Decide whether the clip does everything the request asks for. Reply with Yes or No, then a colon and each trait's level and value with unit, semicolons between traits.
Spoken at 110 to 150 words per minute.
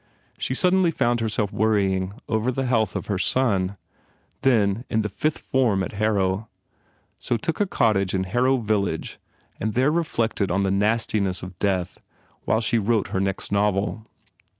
No: average, 165 wpm